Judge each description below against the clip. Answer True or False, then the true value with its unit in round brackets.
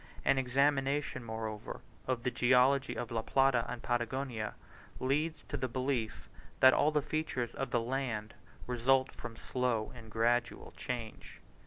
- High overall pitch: False (125 Hz)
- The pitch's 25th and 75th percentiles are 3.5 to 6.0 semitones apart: False (2.5 semitones)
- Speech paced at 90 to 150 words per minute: True (145 wpm)